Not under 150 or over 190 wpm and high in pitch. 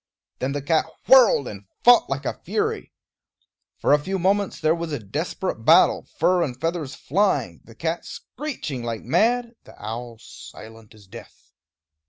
No: average, 160 wpm; medium, 155 Hz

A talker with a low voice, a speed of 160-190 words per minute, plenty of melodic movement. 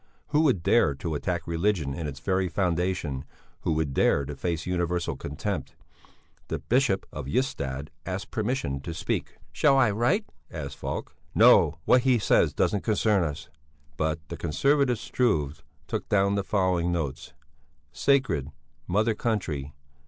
No: very low, 90 Hz; average, 150 wpm; wide, 6.1 semitones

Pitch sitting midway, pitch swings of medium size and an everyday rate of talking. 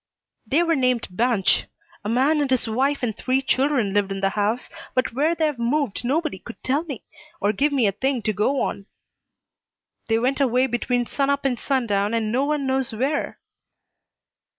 No: very high, 255 Hz; average, 4.0 semitones; average, 190 wpm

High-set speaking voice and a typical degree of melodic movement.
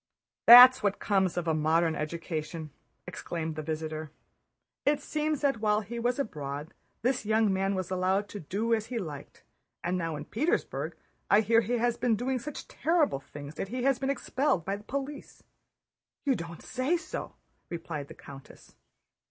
No: high, 205 Hz; wide, 7.4 semitones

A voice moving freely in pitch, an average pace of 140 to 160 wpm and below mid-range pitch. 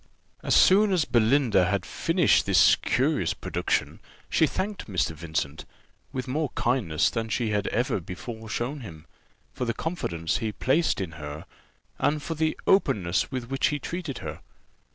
Yes: wide, 8.1 semitones; average, 155 wpm; low, 120 Hz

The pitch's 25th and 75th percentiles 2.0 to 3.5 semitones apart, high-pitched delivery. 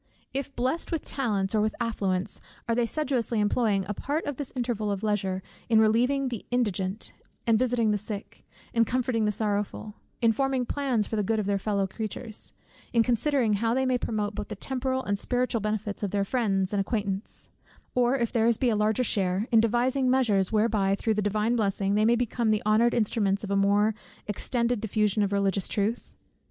Yes: average, 3.0 semitones; high, 220 Hz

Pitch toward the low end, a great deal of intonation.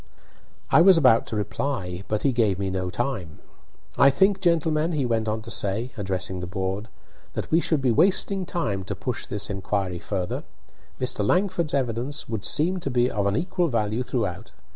Yes: low, 115 Hz; wide, 7.1 semitones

